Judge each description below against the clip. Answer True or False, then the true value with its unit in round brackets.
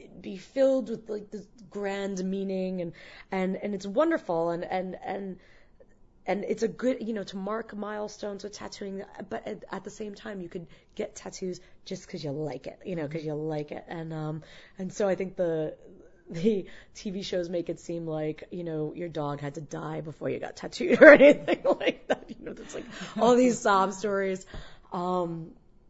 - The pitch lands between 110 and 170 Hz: False (190 Hz)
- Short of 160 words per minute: False (195 wpm)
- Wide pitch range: False (3.4 semitones)